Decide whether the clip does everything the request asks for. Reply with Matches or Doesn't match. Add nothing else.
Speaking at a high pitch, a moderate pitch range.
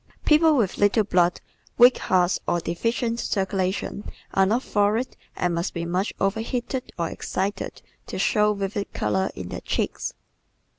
Matches